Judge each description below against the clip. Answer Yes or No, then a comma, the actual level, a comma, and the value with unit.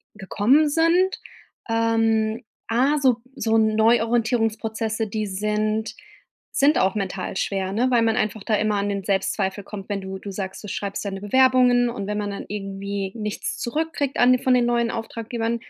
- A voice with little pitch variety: No, average, 3.0 semitones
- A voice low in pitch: No, high, 220 Hz